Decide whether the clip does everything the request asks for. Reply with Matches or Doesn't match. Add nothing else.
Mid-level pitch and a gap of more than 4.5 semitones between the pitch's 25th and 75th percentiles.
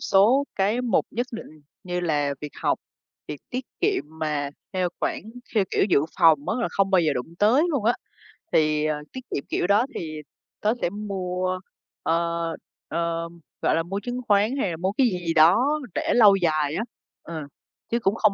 Matches